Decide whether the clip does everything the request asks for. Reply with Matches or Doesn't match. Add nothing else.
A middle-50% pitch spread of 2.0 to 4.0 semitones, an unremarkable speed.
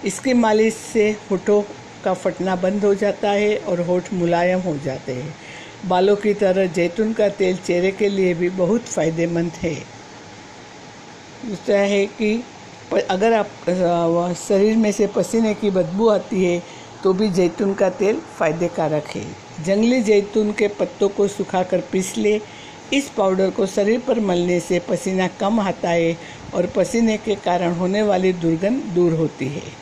Matches